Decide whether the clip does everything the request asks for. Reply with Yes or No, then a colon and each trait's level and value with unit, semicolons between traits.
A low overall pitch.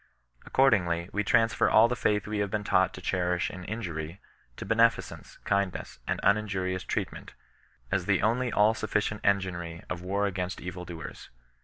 Yes: low, 100 Hz